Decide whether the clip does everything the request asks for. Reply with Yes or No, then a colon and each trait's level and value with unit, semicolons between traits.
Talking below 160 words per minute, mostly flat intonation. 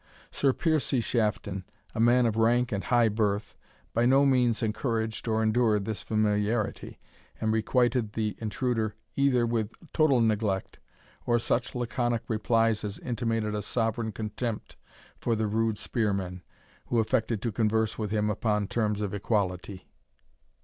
Yes: average, 145 wpm; narrow, 2.1 semitones